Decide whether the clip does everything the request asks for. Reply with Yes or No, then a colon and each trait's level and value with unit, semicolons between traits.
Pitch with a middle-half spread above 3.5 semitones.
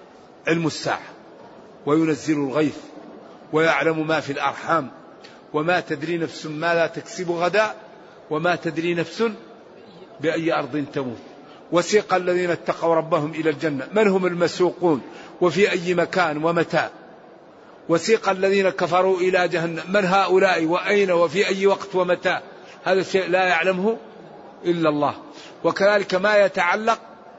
No: average, 2.8 semitones